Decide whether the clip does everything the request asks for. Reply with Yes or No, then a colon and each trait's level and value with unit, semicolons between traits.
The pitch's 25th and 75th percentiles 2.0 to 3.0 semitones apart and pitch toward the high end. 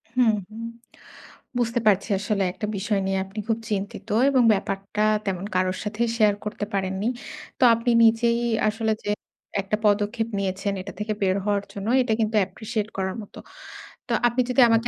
Yes: narrow, 2.5 semitones; high, 210 Hz